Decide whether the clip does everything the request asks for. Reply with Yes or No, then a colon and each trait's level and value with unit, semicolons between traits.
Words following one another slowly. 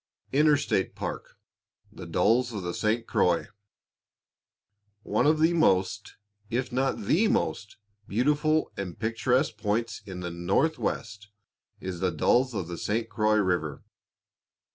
Yes: slow, 125 wpm